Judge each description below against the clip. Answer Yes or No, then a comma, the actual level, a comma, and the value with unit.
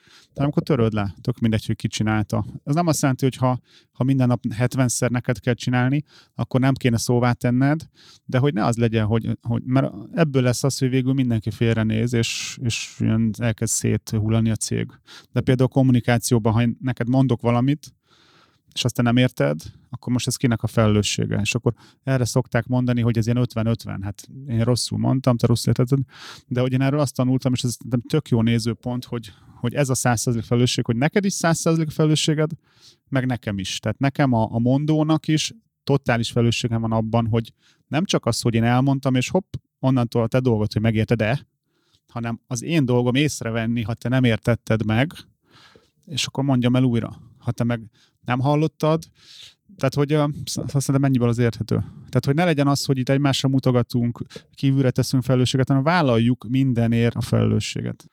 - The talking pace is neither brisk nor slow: No, fast, 185 wpm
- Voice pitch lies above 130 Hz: No, low, 125 Hz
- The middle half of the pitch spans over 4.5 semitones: No, average, 2.7 semitones